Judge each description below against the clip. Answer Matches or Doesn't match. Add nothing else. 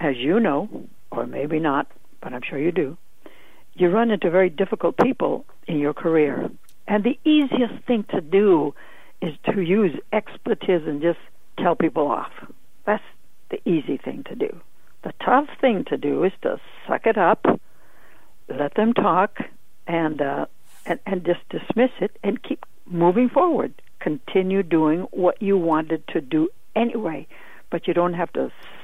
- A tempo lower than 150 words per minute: Doesn't match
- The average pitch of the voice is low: Doesn't match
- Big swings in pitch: Doesn't match